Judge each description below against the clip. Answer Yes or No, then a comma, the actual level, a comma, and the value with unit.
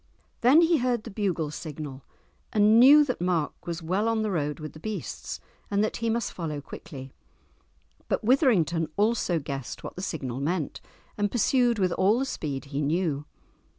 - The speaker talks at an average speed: Yes, average, 175 wpm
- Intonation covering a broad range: Yes, wide, 6.9 semitones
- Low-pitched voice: No, medium, 185 Hz